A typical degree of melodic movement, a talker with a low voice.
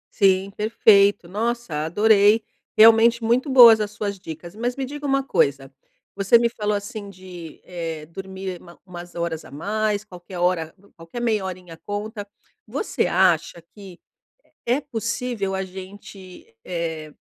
No: average, 4.1 semitones; high, 195 Hz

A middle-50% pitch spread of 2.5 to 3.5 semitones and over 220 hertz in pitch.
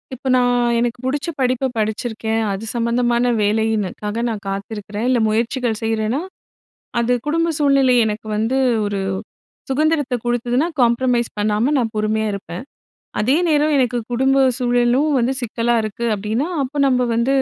Yes: average, 2.9 semitones; high, 240 Hz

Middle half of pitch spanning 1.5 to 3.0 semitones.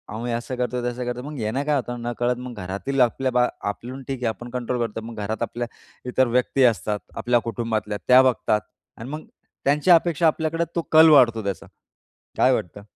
Yes: average, 2.7 semitones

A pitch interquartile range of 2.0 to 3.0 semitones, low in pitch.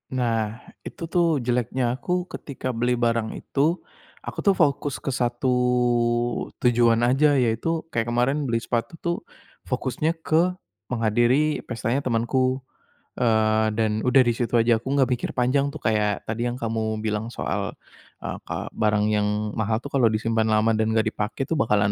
Yes: narrow, 2.6 semitones; low, 120 Hz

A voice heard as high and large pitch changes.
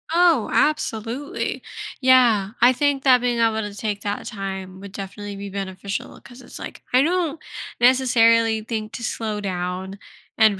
No: high, 220 Hz; average, 4.2 semitones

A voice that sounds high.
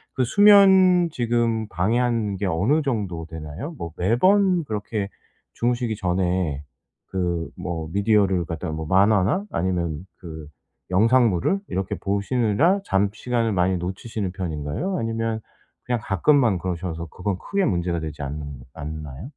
No: low, 100 Hz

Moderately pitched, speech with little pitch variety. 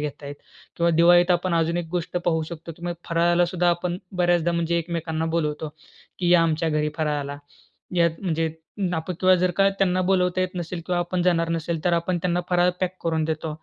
Yes: medium, 170 Hz; narrow, 1.6 semitones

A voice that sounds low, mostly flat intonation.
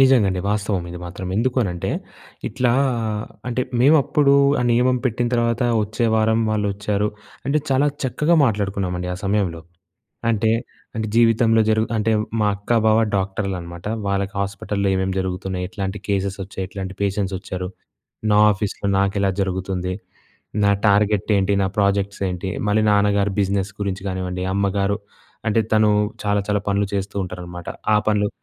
Yes: low, 100 Hz; narrow, 2.3 semitones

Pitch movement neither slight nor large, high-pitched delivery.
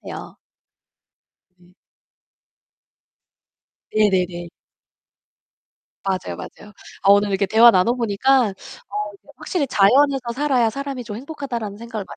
Yes: average, 4.6 semitones; high, 220 Hz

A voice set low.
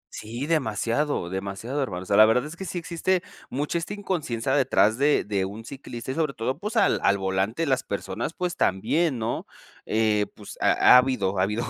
Yes: low, 125 Hz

